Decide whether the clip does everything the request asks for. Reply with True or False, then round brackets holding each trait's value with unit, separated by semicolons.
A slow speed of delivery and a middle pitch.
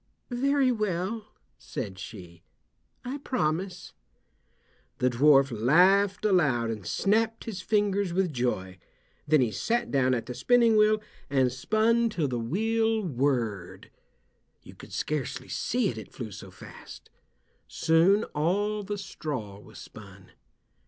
True (130 wpm; 170 Hz)